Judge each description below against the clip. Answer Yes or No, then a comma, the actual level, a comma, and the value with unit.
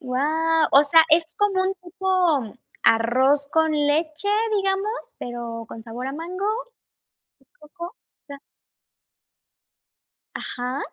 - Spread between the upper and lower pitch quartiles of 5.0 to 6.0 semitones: Yes, wide, 5.6 semitones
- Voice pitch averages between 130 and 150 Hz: No, very high, 310 Hz